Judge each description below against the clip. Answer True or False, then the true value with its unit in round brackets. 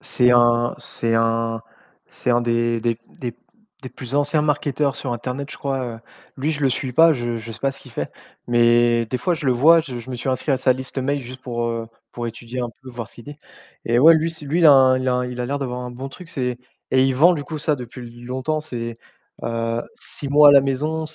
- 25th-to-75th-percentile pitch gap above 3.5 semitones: False (3.0 semitones)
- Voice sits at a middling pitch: False (130 Hz)